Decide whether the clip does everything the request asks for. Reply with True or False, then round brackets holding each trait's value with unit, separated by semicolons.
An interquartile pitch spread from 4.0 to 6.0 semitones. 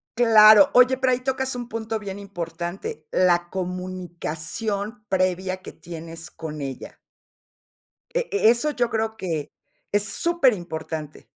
True (4.9 semitones)